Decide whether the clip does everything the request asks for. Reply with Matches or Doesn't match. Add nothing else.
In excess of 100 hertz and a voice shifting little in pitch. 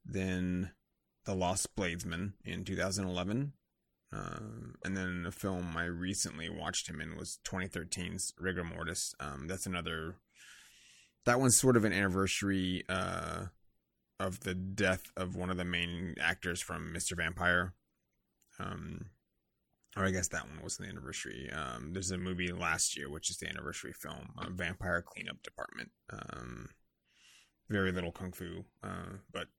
Doesn't match